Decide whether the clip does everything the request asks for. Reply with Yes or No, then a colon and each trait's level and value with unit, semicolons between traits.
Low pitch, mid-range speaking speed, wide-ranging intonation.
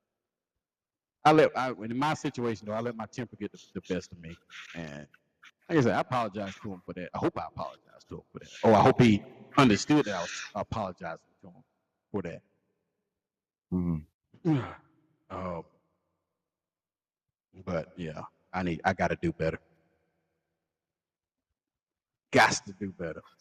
Yes: low, 100 Hz; average, 160 wpm; wide, 6.2 semitones